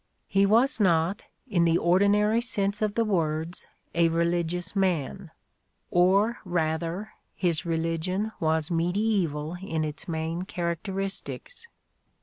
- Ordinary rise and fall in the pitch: Yes, average, 3.5 semitones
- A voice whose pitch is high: No, medium, 175 Hz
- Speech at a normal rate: No, slow, 115 wpm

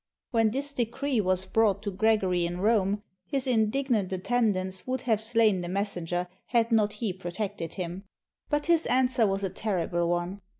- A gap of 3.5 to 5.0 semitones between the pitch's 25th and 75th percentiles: Yes, average, 3.9 semitones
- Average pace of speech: Yes, average, 165 wpm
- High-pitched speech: Yes, high, 210 Hz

